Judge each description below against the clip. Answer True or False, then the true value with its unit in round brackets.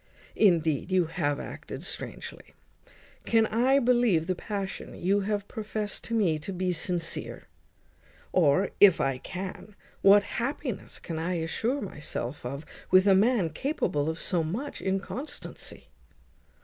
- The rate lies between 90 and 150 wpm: True (135 wpm)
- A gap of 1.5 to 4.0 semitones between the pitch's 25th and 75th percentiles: False (4.8 semitones)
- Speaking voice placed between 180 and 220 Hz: True (190 Hz)